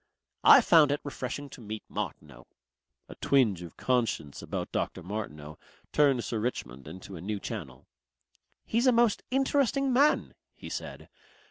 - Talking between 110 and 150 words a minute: Yes, average, 145 wpm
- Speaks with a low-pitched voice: Yes, low, 120 Hz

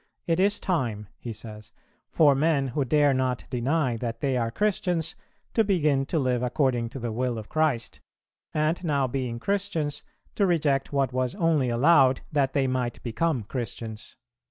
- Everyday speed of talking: Yes, average, 165 wpm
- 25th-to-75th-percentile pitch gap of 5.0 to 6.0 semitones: No, average, 4.6 semitones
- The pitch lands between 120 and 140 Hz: Yes, low, 135 Hz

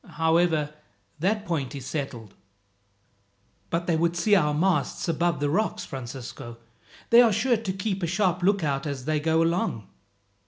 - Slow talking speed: No, average, 155 wpm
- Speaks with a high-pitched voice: No, medium, 165 Hz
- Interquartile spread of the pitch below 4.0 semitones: No, average, 4.5 semitones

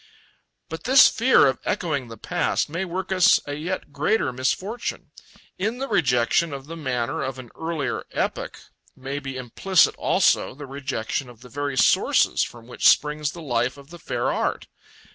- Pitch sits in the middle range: Yes, medium, 145 Hz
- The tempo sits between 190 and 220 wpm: No, average, 170 wpm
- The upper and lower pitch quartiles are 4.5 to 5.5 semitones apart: Yes, average, 5.0 semitones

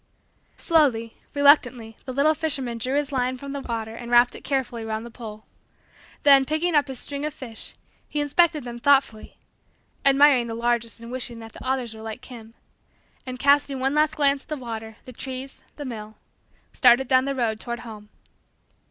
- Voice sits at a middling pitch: No, very high, 255 Hz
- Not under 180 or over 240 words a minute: Yes, average, 185 wpm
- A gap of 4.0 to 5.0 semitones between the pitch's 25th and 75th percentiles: No, average, 3.4 semitones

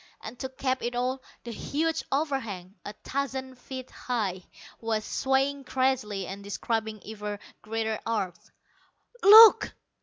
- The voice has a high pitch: Yes, high, 240 Hz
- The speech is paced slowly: Yes, slow, 125 wpm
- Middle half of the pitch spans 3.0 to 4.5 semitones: Yes, average, 3.9 semitones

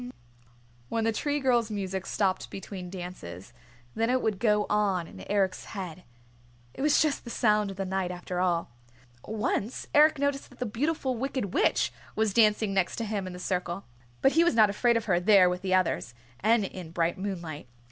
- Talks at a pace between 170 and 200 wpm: Yes, average, 190 wpm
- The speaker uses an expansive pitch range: No, average, 3.9 semitones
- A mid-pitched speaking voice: No, high, 200 Hz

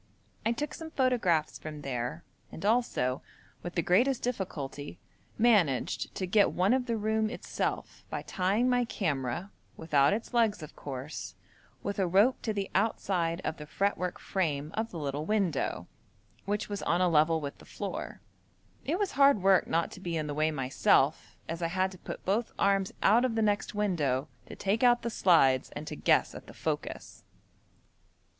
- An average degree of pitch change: No, wide, 6.0 semitones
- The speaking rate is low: No, average, 180 wpm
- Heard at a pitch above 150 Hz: Yes, high, 190 Hz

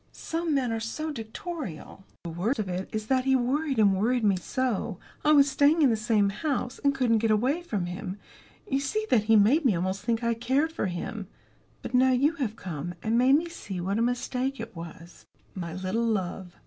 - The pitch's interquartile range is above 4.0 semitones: Yes, wide, 5.6 semitones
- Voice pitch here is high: Yes, high, 230 Hz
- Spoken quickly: Yes, fast, 210 wpm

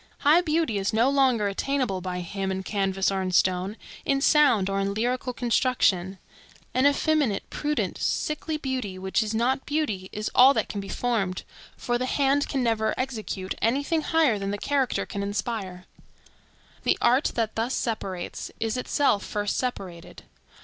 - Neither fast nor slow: Yes, average, 165 wpm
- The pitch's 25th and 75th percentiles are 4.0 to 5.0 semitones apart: No, wide, 5.4 semitones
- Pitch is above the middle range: Yes, high, 225 Hz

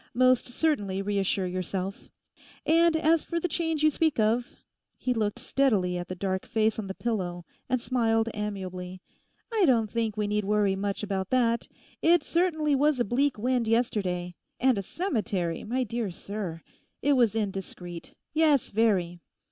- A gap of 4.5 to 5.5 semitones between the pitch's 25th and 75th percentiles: Yes, average, 5.1 semitones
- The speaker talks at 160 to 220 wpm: No, average, 150 wpm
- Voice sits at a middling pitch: No, high, 220 Hz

